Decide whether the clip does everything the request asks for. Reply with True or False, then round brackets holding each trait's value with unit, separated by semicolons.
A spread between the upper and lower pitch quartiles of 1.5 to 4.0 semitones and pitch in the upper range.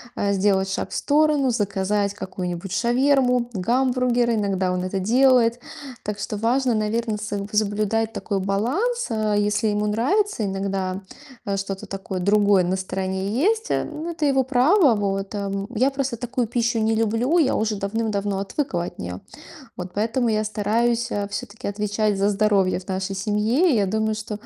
True (3.6 semitones; 215 Hz)